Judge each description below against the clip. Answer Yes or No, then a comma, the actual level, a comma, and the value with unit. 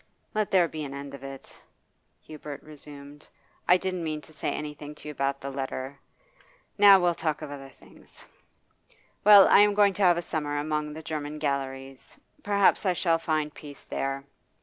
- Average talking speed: Yes, average, 180 wpm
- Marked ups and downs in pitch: No, average, 3.6 semitones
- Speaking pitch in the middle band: Yes, medium, 150 Hz